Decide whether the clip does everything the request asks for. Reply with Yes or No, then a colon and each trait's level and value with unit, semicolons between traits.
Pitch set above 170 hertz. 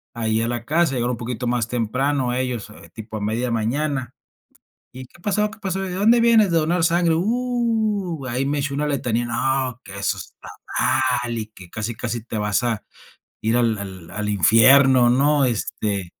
No: low, 125 Hz